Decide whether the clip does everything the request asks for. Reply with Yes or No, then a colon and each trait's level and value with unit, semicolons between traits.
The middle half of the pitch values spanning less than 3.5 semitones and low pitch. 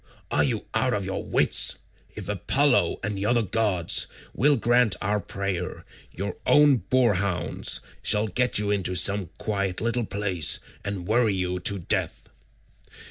No: average, 3.9 semitones; low, 100 Hz